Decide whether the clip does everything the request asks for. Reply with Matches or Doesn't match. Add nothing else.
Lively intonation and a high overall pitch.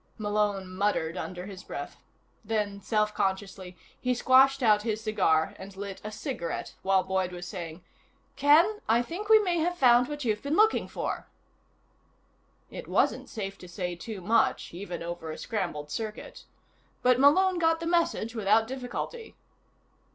Matches